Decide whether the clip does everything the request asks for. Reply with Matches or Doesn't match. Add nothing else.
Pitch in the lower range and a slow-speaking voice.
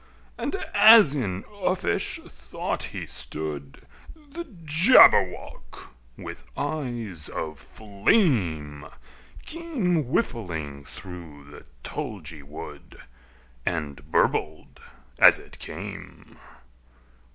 Matches